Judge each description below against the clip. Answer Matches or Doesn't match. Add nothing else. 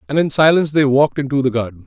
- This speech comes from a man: Matches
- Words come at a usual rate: Doesn't match